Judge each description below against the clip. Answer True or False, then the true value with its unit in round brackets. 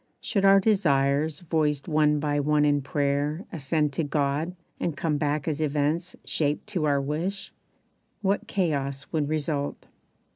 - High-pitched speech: False (150 Hz)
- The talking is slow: False (145 wpm)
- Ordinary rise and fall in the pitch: False (2.3 semitones)